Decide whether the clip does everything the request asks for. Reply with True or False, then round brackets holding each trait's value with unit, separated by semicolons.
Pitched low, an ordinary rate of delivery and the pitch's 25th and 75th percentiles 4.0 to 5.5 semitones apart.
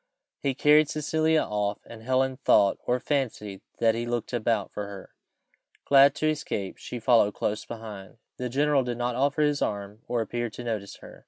True (120 Hz; 180 wpm; 4.6 semitones)